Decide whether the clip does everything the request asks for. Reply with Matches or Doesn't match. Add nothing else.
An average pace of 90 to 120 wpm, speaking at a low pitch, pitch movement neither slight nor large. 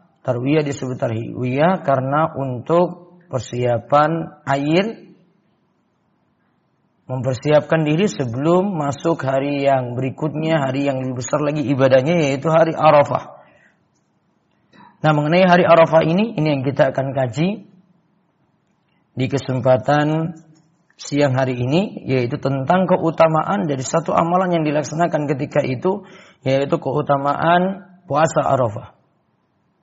Doesn't match